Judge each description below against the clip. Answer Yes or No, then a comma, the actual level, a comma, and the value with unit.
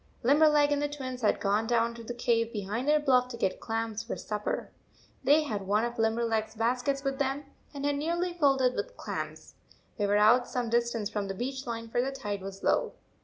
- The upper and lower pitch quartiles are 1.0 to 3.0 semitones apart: No, average, 3.7 semitones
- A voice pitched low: No, high, 240 Hz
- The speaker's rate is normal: No, fast, 220 wpm